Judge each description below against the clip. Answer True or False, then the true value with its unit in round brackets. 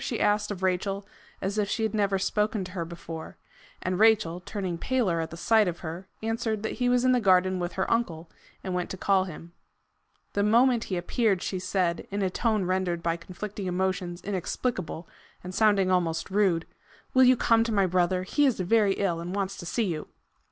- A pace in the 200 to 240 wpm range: True (205 wpm)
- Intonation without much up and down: False (3.2 semitones)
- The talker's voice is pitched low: False (190 Hz)